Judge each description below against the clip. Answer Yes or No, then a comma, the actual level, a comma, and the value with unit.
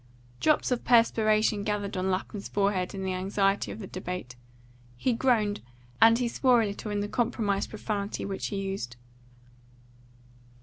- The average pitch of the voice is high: Yes, high, 205 Hz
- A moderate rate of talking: Yes, average, 150 wpm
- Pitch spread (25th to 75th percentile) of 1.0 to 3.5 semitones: Yes, narrow, 2.5 semitones